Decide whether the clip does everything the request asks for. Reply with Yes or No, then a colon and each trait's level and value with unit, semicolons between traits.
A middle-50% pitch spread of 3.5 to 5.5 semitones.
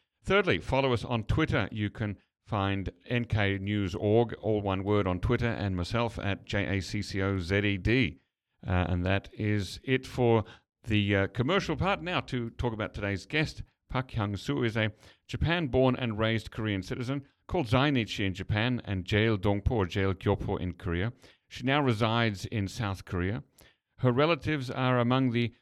Yes: average, 3.9 semitones